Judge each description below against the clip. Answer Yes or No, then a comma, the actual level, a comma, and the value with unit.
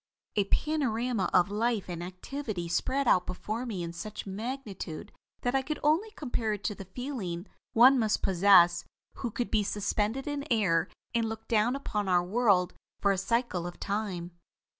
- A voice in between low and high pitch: No, high, 210 Hz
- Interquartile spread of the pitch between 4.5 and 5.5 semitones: Yes, average, 5.0 semitones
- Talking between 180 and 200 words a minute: No, average, 170 wpm